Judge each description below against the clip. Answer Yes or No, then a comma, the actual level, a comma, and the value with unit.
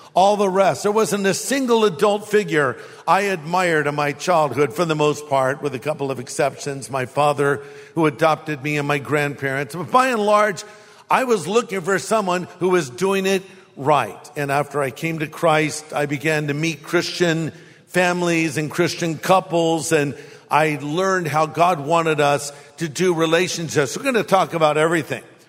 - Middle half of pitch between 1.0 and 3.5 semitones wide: No, average, 4.0 semitones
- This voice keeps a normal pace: Yes, average, 180 wpm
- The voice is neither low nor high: Yes, medium, 160 Hz